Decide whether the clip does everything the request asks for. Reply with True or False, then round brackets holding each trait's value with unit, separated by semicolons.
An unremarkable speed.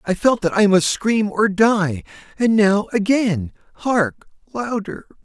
False (125 wpm)